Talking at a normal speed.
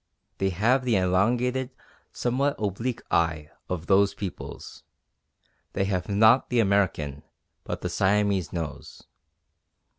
No: slow, 115 wpm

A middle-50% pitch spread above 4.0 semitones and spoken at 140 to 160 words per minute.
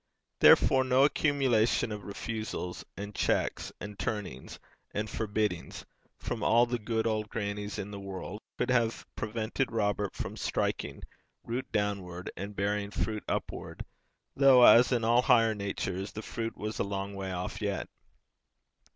No: narrow, 2.5 semitones; average, 145 wpm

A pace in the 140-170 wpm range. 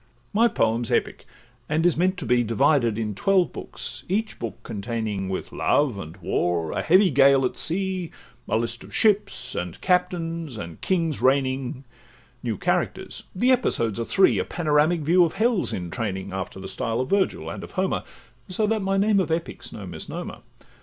No: average, 185 wpm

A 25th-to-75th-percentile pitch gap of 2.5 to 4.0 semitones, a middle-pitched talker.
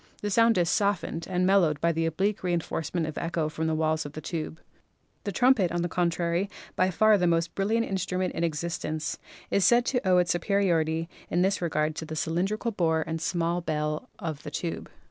Yes: average, 3.1 semitones; medium, 170 Hz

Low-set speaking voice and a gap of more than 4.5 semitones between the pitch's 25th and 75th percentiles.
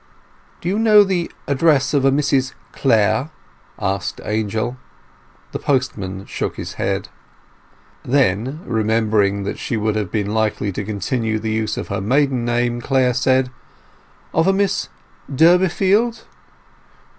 Yes: low, 120 Hz; average, 5.1 semitones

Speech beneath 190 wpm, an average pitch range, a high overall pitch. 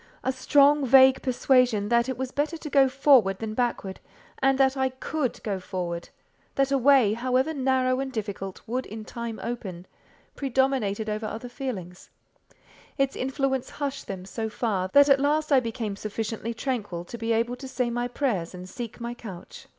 Yes: average, 170 wpm; average, 3.8 semitones; high, 245 Hz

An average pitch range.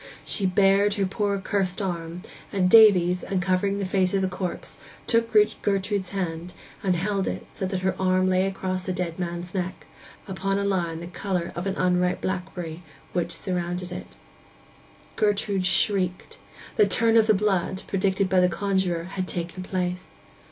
No: narrow, 1.6 semitones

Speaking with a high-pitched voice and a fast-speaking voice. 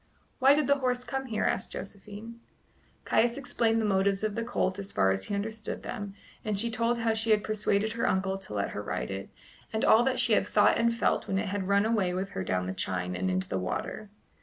Yes: high, 205 Hz; fast, 235 wpm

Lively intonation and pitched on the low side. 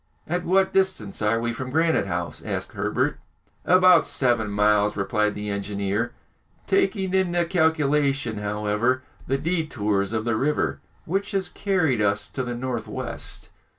Yes: wide, 8.5 semitones; low, 130 Hz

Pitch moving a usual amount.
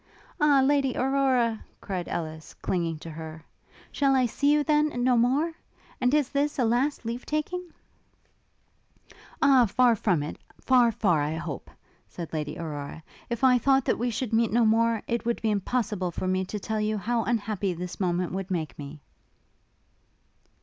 No: wide, 6.4 semitones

